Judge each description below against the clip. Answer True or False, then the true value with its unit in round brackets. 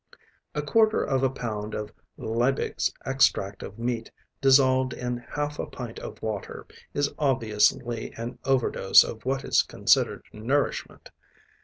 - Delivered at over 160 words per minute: False (140 wpm)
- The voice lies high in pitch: False (125 Hz)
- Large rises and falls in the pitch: False (3.3 semitones)